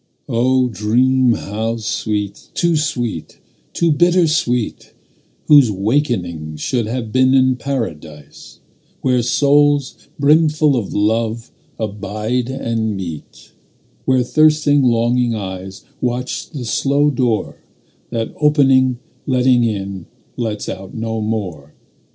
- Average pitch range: Yes, average, 4.0 semitones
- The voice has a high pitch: No, low, 120 Hz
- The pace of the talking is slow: Yes, slow, 110 wpm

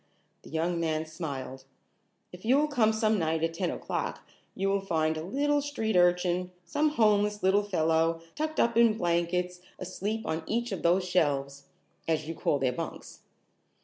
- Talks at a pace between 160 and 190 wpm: Yes, average, 170 wpm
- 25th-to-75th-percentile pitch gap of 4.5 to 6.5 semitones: Yes, average, 5.2 semitones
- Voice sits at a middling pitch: Yes, medium, 180 Hz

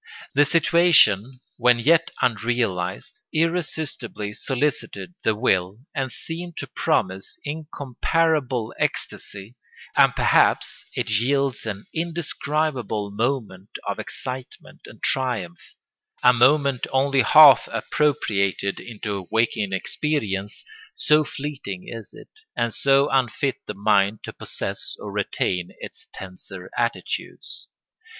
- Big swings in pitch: Yes, wide, 6.1 semitones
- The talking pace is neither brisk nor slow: No, slow, 105 wpm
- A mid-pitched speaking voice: No, low, 125 Hz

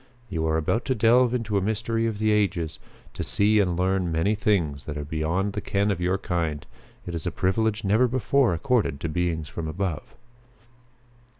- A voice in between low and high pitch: No, very low, 95 Hz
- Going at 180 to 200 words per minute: Yes, average, 190 wpm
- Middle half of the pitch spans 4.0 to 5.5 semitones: Yes, average, 4.8 semitones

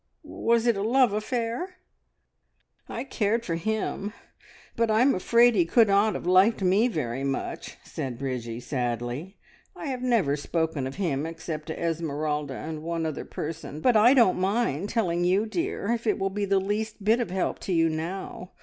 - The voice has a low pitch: No, high, 190 Hz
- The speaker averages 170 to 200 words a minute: Yes, average, 180 wpm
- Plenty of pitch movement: Yes, wide, 6.2 semitones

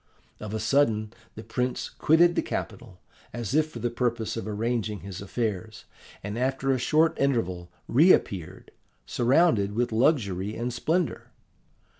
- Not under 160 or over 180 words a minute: No, average, 140 wpm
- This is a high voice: No, low, 115 Hz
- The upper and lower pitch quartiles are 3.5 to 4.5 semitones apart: Yes, average, 4.2 semitones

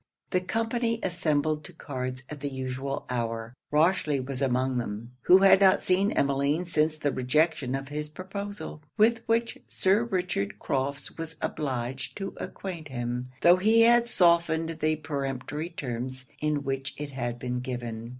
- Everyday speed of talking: Yes, average, 155 wpm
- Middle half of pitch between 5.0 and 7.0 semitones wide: Yes, wide, 5.6 semitones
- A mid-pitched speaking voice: Yes, medium, 150 Hz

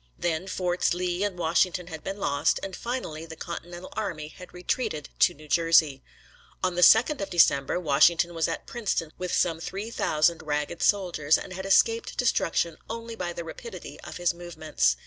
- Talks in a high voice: No, medium, 175 Hz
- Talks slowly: No, average, 175 wpm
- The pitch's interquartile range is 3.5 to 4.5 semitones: No, average, 3.1 semitones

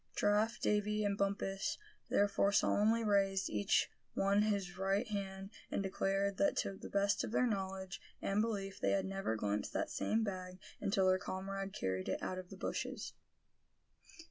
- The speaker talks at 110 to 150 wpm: No, average, 165 wpm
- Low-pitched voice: No, high, 195 Hz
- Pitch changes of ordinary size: No, narrow, 1.2 semitones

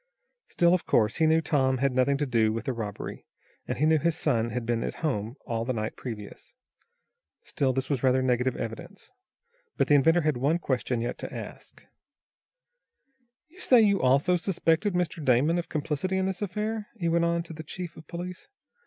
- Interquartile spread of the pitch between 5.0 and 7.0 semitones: Yes, wide, 5.5 semitones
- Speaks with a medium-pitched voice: Yes, medium, 145 Hz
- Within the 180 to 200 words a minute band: Yes, average, 195 wpm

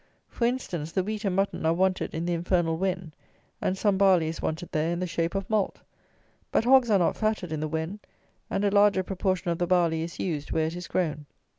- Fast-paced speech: Yes, fast, 230 wpm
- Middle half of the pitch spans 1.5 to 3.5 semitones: Yes, average, 3.1 semitones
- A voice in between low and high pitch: Yes, medium, 180 Hz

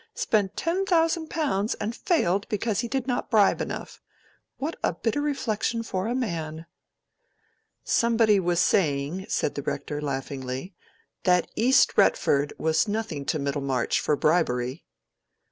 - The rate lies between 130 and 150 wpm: Yes, slow, 135 wpm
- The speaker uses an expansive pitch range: Yes, wide, 7.9 semitones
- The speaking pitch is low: No, high, 195 Hz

